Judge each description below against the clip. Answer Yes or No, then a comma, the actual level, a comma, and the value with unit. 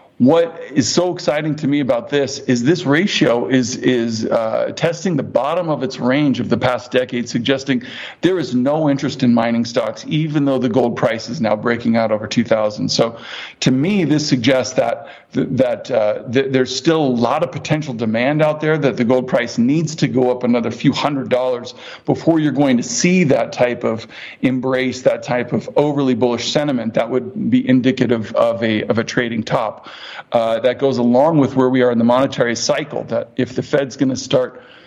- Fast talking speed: Yes, fast, 210 wpm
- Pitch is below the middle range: Yes, low, 130 Hz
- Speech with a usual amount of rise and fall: Yes, average, 3.4 semitones